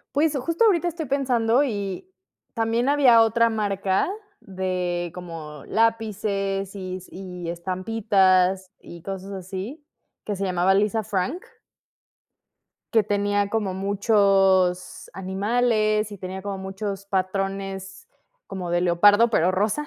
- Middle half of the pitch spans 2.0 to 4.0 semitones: Yes, average, 3.1 semitones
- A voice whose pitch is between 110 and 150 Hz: No, high, 195 Hz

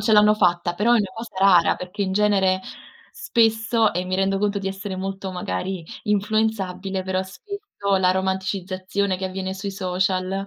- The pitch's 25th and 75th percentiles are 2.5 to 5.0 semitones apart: No, narrow, 1.9 semitones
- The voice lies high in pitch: Yes, high, 195 Hz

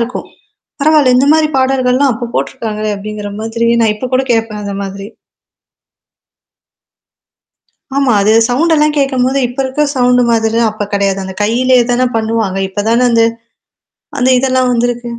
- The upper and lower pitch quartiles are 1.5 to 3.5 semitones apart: Yes, average, 3.1 semitones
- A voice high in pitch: Yes, high, 240 Hz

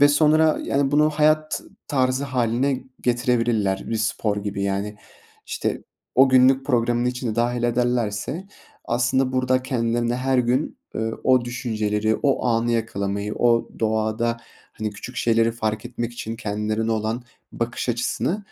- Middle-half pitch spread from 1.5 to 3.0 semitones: Yes, narrow, 2.6 semitones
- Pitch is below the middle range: Yes, low, 120 Hz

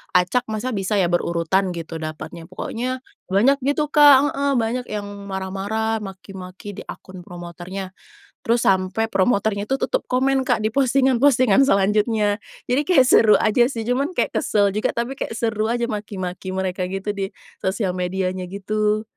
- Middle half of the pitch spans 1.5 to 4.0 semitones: No, average, 4.6 semitones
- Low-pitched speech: No, high, 210 Hz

